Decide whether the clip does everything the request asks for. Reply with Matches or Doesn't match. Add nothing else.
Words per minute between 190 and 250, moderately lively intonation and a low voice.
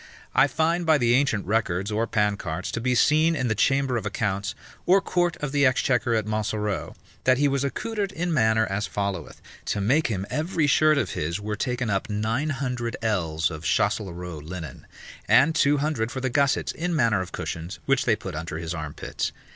Doesn't match